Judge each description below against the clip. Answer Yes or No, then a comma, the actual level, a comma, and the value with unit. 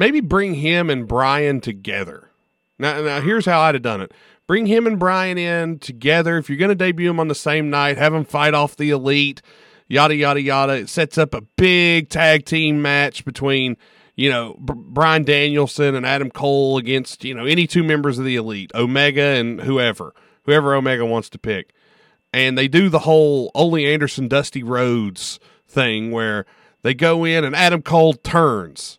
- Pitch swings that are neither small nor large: Yes, average, 3.4 semitones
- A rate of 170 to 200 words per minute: Yes, average, 185 wpm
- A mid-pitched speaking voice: Yes, medium, 145 Hz